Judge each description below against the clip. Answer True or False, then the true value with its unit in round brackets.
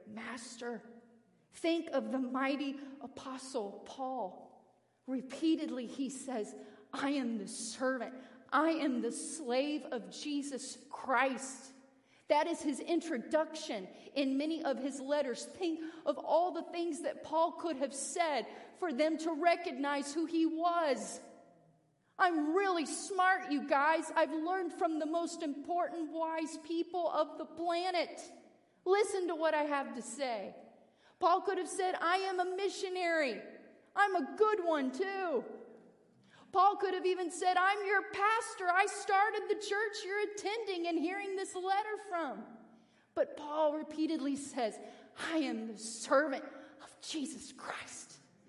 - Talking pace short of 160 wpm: True (140 wpm)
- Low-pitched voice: False (315 Hz)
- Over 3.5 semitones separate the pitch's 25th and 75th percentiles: True (4.5 semitones)